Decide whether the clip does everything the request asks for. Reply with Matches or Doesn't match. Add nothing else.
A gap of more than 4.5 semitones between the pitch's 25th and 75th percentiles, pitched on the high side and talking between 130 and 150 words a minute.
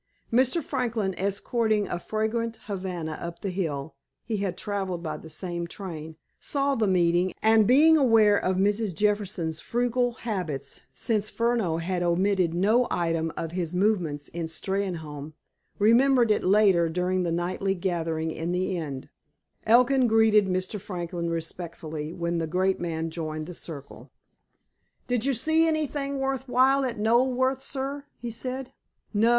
Matches